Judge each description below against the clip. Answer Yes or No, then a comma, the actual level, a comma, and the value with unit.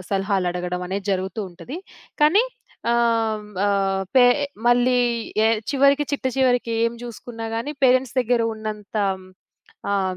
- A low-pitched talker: No, high, 230 Hz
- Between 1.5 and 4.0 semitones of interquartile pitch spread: No, average, 4.4 semitones